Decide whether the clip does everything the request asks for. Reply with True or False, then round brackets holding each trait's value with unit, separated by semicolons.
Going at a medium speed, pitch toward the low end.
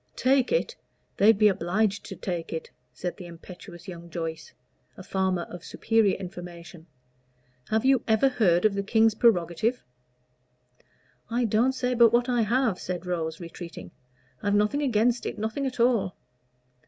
False (155 wpm; 205 Hz)